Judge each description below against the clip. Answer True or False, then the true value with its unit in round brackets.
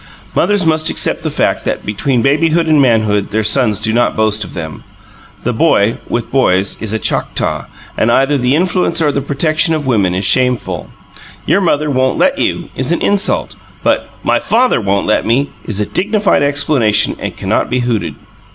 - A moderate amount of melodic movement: False (6.3 semitones)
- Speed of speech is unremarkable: True (185 wpm)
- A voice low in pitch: True (130 Hz)